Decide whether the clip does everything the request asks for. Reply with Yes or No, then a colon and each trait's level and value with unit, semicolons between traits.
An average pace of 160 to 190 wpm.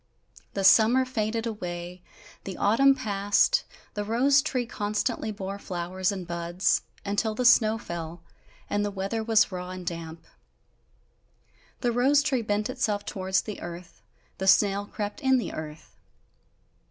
No: average, 140 wpm